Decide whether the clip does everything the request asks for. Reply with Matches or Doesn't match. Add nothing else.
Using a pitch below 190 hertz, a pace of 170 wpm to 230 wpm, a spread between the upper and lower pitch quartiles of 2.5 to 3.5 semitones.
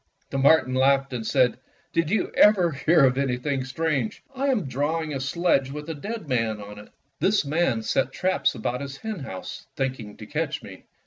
Doesn't match